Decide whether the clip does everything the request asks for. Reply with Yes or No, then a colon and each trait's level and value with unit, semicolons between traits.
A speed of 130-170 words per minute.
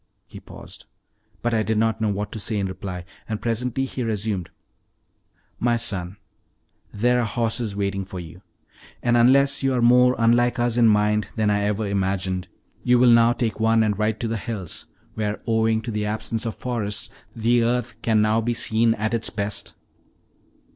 No: average, 180 wpm